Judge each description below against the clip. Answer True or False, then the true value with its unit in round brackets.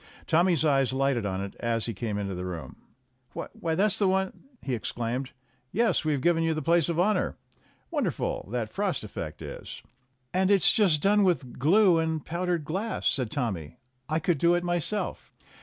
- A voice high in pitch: False (160 Hz)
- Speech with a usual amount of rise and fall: False (7.0 semitones)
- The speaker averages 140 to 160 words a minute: False (190 wpm)